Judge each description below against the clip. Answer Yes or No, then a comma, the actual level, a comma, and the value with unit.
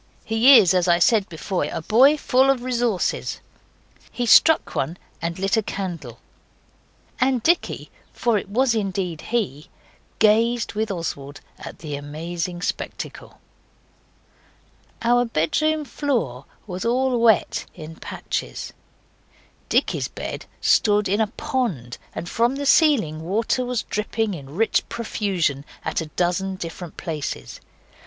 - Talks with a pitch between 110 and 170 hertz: No, high, 205 Hz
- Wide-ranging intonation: Yes, wide, 6.1 semitones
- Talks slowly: Yes, slow, 130 wpm